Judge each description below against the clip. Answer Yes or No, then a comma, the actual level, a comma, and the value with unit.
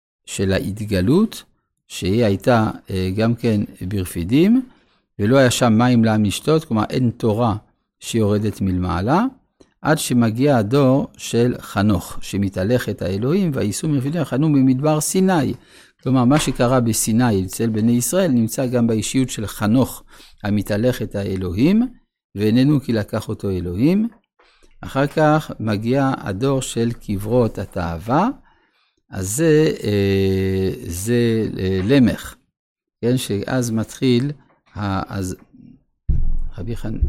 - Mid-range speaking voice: No, low, 115 Hz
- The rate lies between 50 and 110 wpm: Yes, average, 105 wpm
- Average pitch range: Yes, average, 5.0 semitones